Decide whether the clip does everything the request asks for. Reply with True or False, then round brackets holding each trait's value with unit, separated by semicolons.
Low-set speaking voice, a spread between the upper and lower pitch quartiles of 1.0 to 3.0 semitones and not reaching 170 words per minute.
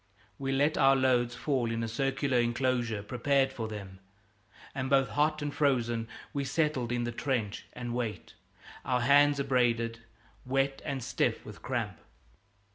True (130 Hz; 2.6 semitones; 150 wpm)